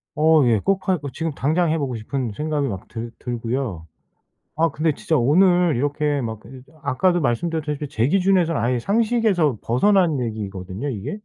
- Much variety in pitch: Yes, wide, 5.9 semitones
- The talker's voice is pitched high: No, medium, 145 Hz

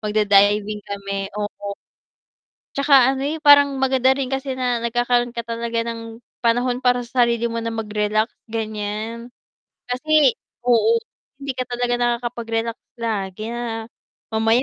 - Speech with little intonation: Yes, narrow, 2.3 semitones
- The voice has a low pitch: No, high, 235 Hz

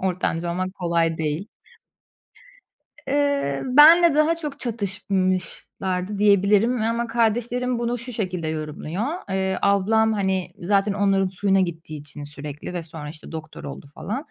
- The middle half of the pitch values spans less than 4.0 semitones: No, average, 5.2 semitones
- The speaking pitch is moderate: No, high, 195 Hz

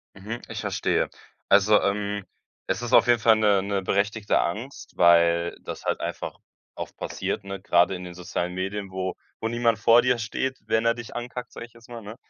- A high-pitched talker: No, low, 105 Hz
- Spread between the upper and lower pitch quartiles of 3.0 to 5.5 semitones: Yes, average, 3.5 semitones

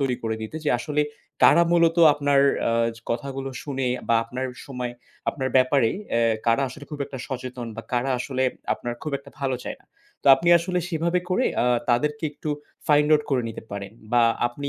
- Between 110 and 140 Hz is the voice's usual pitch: Yes, low, 135 Hz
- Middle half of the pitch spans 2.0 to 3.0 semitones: No, average, 3.4 semitones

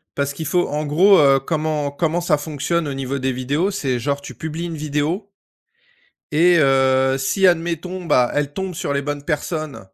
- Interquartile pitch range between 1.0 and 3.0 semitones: No, average, 3.4 semitones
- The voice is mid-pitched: Yes, medium, 150 Hz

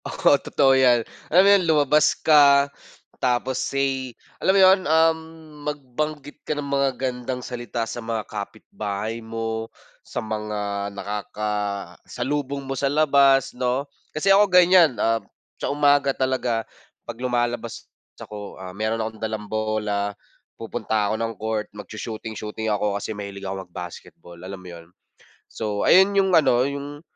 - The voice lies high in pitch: No, low, 120 Hz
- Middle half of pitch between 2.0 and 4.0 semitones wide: No, average, 4.8 semitones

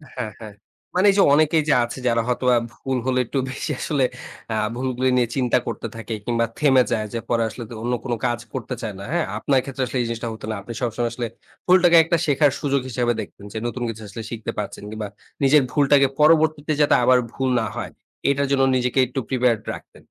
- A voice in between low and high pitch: No, low, 125 Hz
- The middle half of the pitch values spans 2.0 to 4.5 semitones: Yes, average, 3.3 semitones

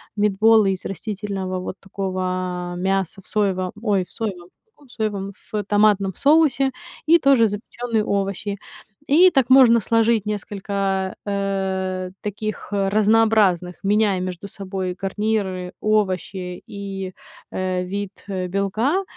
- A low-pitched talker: No, high, 200 Hz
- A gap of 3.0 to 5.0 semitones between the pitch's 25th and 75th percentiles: No, narrow, 2.5 semitones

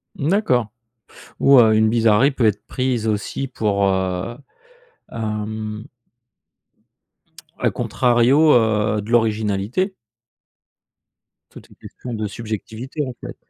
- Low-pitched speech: Yes, low, 110 Hz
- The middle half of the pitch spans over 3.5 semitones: No, average, 2.9 semitones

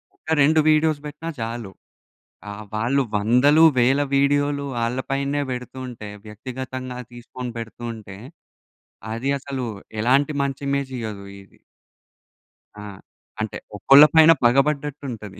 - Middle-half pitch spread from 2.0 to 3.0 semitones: No, average, 3.5 semitones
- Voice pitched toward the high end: No, low, 130 Hz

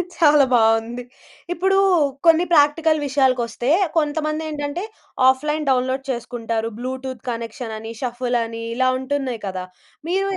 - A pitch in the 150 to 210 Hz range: No, very high, 260 Hz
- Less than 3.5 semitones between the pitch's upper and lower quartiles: No, average, 4.0 semitones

